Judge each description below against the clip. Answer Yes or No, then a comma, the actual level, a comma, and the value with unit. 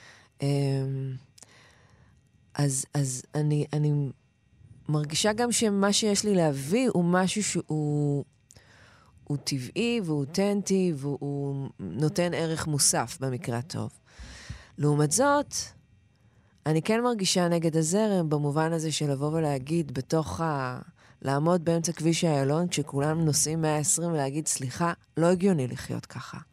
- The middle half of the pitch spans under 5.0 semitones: Yes, average, 4.2 semitones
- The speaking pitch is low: No, medium, 150 Hz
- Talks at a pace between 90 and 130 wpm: Yes, average, 115 wpm